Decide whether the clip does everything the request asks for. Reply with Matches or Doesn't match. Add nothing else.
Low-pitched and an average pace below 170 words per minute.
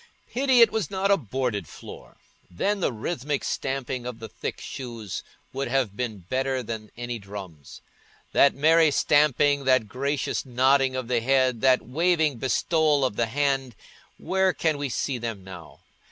Matches